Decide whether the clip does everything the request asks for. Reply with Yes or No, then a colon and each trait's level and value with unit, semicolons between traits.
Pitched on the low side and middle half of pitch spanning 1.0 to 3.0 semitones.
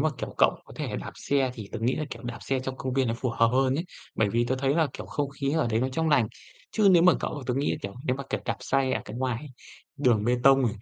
Yes: low, 130 Hz; narrow, 2.6 semitones